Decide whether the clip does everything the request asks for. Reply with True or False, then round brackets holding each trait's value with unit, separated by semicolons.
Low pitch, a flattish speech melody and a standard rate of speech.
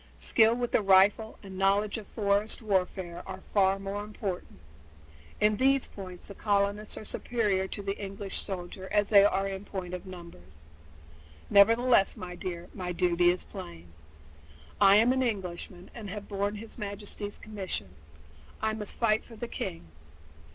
False (200 Hz; 2.3 semitones; 165 wpm)